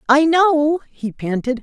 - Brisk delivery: No, average, 150 wpm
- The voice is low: No, very high, 285 Hz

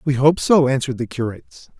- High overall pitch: No, low, 135 Hz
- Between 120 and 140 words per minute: No, average, 200 wpm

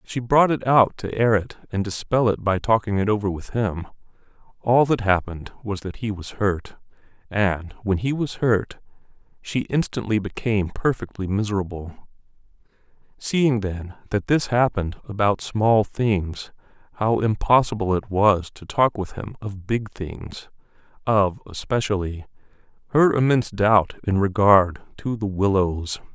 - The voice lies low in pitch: Yes, low, 105 Hz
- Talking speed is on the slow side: No, average, 145 wpm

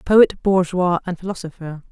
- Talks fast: No, slow, 125 wpm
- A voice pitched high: No, medium, 180 Hz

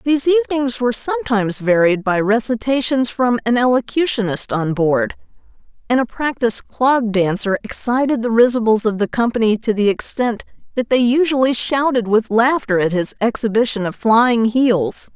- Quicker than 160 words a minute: No, average, 150 wpm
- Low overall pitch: No, high, 230 Hz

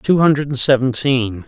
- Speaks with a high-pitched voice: No, low, 130 Hz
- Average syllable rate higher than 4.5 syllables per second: No, 4.2 syllables/s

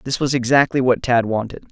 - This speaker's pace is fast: Yes, fast, 210 wpm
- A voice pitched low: Yes, low, 125 Hz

